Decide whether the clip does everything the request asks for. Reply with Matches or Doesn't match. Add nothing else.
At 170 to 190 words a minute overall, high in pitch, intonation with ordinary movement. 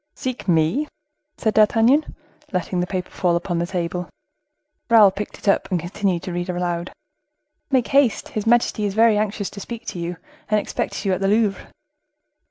Matches